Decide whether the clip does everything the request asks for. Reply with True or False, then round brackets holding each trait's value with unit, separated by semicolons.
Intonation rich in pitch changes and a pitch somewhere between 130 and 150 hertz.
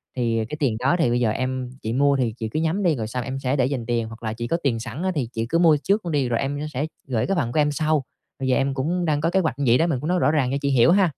False (4.6 semitones; 135 Hz)